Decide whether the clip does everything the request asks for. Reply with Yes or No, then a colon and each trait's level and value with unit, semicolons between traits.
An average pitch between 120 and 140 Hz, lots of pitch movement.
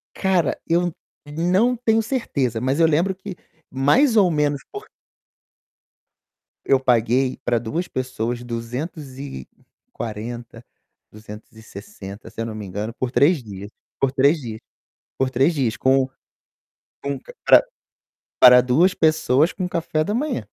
Yes: low, 135 Hz; wide, 6.5 semitones